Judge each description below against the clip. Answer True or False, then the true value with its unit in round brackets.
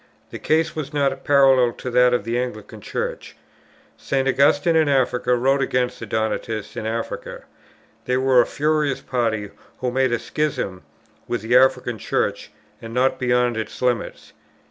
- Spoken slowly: False (160 wpm)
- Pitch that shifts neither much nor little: False (2.3 semitones)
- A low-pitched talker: True (125 Hz)